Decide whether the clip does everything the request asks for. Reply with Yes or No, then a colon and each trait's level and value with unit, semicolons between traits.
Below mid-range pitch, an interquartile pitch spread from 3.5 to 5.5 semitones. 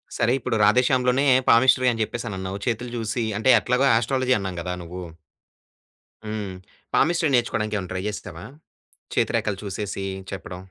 Yes: low, 110 Hz; average, 4.4 semitones